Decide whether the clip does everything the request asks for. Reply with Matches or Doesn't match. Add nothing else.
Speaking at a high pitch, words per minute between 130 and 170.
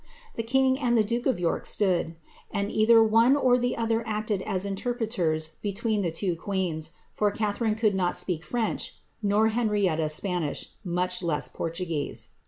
Matches